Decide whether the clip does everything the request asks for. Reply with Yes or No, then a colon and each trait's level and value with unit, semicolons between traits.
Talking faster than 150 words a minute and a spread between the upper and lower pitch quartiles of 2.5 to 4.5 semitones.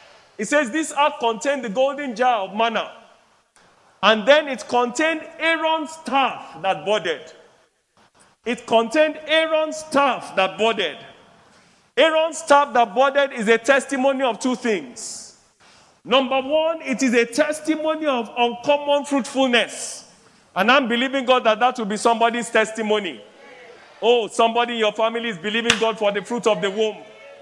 No: average, 145 wpm; average, 4.2 semitones